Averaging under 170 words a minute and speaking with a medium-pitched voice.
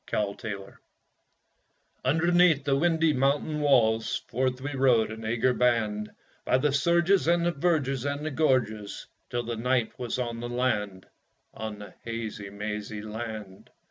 No: average, 150 wpm; low, 125 Hz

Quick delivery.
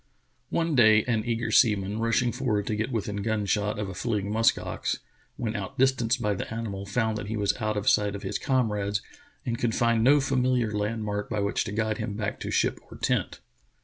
Yes: fast, 210 wpm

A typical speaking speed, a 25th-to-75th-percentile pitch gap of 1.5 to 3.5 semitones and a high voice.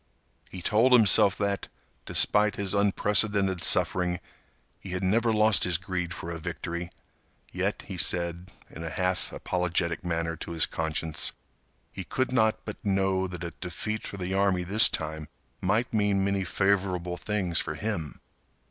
No: average, 155 wpm; average, 2.9 semitones; very low, 95 Hz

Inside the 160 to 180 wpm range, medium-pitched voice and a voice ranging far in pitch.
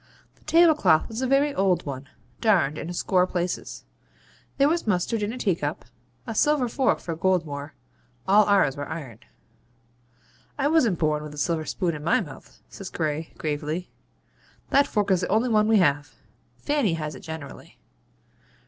Yes: average, 165 wpm; medium, 180 Hz; wide, 6.5 semitones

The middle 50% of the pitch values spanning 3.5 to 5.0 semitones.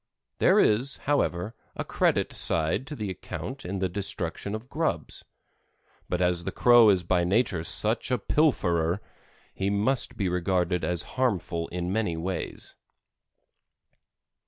Yes: average, 4.5 semitones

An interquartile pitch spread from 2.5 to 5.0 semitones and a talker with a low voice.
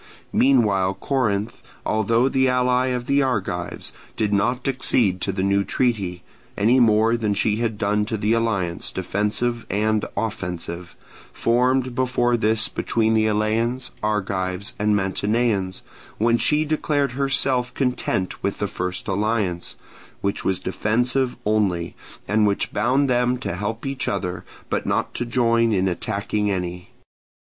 Yes: average, 3.7 semitones; low, 110 Hz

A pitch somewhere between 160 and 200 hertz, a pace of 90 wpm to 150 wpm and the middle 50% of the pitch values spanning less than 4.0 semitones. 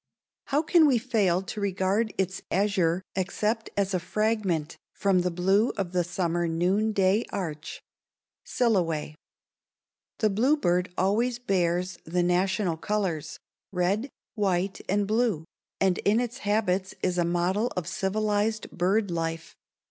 Yes: high, 190 Hz; slow, 135 wpm; average, 3.3 semitones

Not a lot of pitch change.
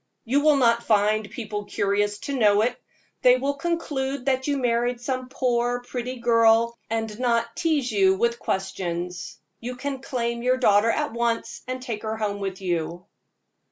No: average, 3.4 semitones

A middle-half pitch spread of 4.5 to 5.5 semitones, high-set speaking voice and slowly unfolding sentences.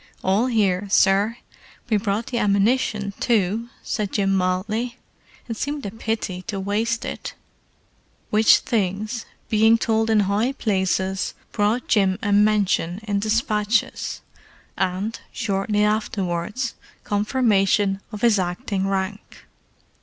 No: narrow, 2.5 semitones; high, 210 Hz; slow, 115 wpm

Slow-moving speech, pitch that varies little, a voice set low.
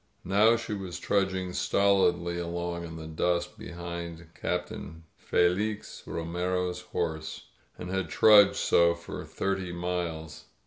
Yes: slow, 130 wpm; narrow, 2.0 semitones; very low, 90 Hz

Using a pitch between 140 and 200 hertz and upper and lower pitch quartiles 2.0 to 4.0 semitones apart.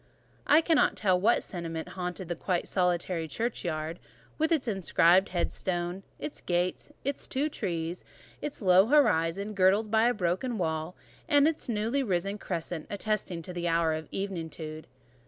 No: medium, 185 Hz; average, 4.4 semitones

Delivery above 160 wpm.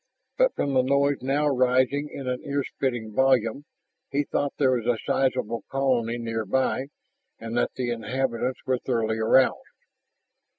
No: average, 145 wpm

